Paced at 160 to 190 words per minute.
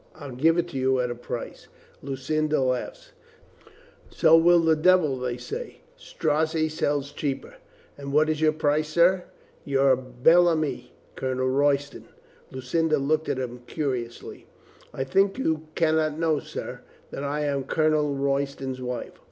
No: average, 145 wpm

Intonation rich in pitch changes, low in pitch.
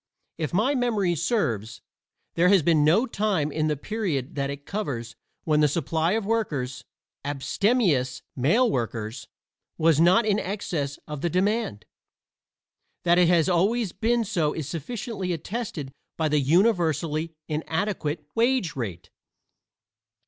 No: wide, 6.1 semitones; medium, 165 Hz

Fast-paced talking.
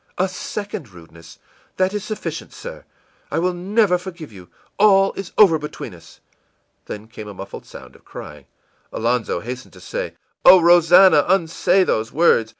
No: average, 160 wpm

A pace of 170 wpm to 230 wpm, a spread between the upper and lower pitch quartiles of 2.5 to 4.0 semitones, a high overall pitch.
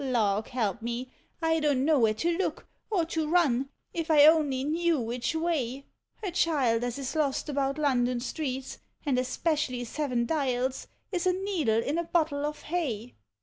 No: average, 180 wpm; average, 4.6 semitones; very high, 280 Hz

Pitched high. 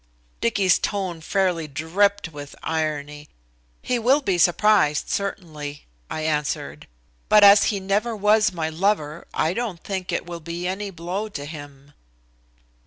No: medium, 175 Hz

